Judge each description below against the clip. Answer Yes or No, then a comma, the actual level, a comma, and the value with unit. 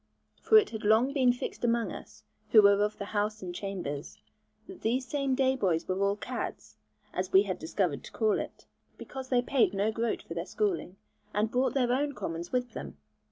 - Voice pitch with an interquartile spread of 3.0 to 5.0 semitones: Yes, average, 4.5 semitones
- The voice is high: Yes, high, 220 Hz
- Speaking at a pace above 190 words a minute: Yes, fast, 205 wpm